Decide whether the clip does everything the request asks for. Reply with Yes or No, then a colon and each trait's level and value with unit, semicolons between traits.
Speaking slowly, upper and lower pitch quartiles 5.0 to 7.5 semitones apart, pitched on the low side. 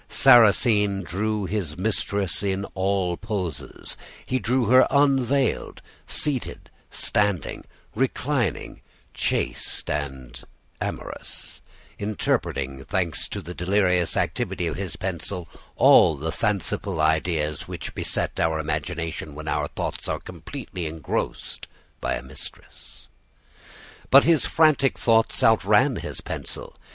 Yes: slow, 110 wpm; wide, 5.5 semitones; very low, 95 Hz